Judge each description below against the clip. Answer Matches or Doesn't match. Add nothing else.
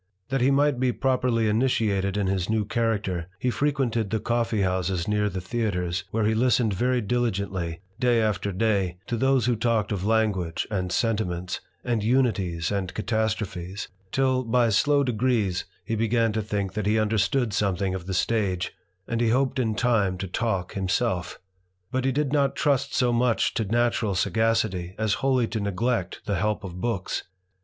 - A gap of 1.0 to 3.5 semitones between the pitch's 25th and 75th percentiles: Doesn't match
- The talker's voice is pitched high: Doesn't match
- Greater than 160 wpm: Matches